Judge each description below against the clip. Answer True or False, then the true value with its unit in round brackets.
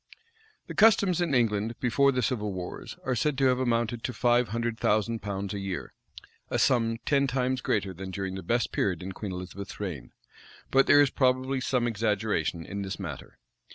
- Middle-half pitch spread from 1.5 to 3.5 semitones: False (4.6 semitones)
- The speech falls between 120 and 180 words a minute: False (190 wpm)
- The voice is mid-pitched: False (115 Hz)